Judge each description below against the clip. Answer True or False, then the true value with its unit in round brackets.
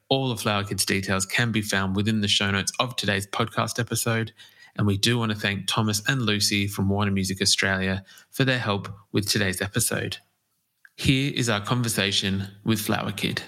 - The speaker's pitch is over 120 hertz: False (105 Hz)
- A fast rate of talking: False (185 wpm)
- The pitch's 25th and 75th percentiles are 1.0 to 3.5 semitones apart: True (2.6 semitones)